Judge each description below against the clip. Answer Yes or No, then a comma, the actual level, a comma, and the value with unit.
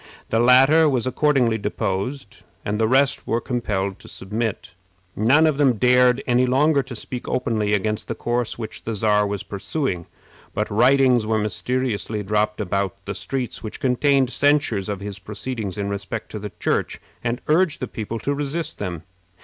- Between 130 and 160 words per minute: No, average, 170 wpm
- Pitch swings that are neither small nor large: Yes, average, 4.1 semitones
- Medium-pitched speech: No, low, 115 Hz